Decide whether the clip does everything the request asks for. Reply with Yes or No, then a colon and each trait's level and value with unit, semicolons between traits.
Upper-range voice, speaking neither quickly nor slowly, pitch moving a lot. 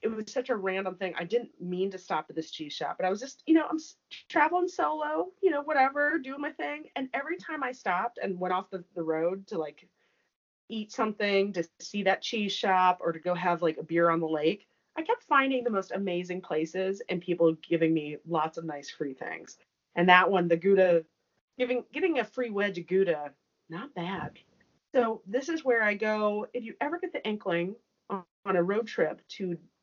No: high, 195 Hz; fast, 215 wpm; wide, 6.4 semitones